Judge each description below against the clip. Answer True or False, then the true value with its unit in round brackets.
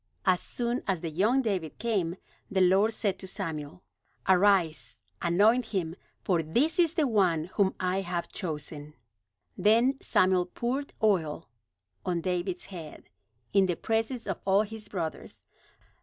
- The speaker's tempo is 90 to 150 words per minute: True (140 wpm)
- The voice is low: False (190 Hz)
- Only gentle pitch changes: False (4.3 semitones)